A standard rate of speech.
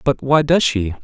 No: fast, 230 wpm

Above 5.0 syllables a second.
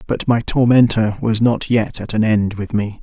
No: 4.6 syllables/s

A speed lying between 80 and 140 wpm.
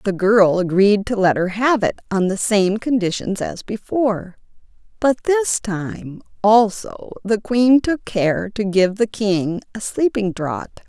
No: average, 160 wpm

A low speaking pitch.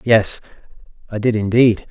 Yes: low, 110 Hz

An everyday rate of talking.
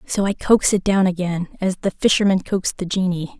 No: fast, 210 wpm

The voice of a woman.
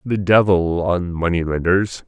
No: male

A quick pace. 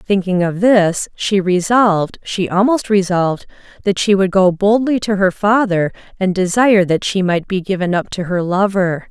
No: average, 165 wpm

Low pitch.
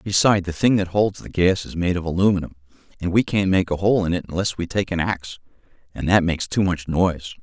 Yes: very low, 90 Hz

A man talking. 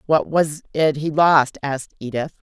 No: female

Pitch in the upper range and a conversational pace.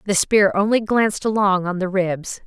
Yes: high, 195 Hz; average, 195 wpm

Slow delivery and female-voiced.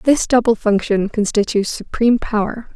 Yes: slow, 130 wpm; female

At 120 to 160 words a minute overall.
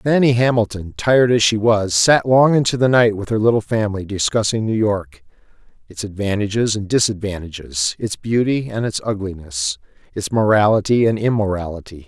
Yes: average, 150 wpm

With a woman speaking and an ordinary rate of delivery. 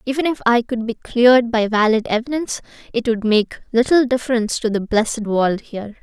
Yes: female; average, 190 wpm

